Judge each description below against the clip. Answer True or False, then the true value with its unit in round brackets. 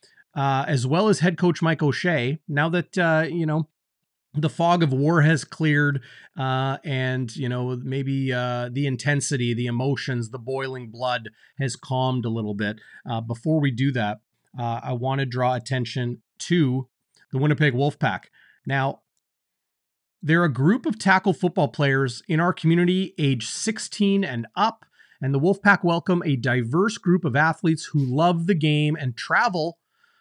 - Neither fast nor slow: True (165 wpm)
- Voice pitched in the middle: True (145 Hz)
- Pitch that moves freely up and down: False (4.7 semitones)